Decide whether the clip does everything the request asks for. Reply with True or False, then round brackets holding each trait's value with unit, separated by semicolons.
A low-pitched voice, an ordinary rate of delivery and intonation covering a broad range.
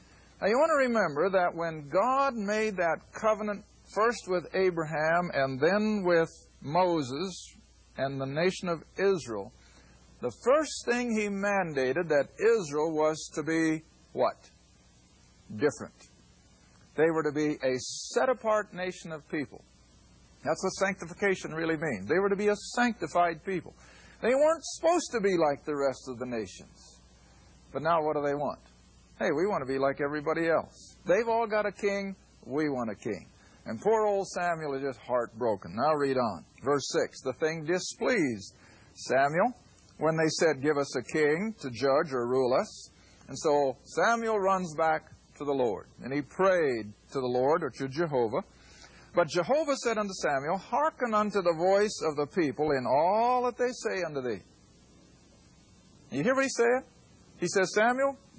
False (165 Hz; 170 wpm; 7.0 semitones)